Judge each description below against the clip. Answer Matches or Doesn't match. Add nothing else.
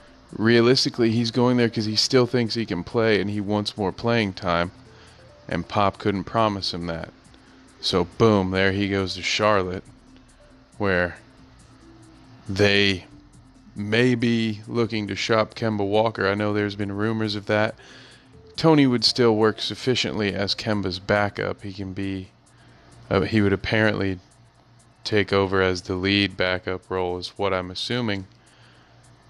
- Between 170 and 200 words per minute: Doesn't match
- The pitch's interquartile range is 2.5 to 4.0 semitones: Matches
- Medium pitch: Doesn't match